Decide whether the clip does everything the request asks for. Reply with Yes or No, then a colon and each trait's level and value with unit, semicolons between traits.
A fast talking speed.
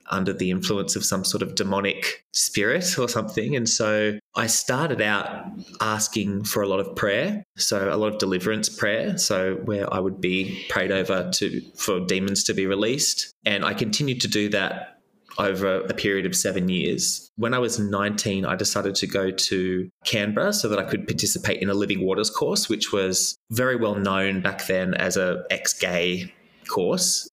No: average, 185 wpm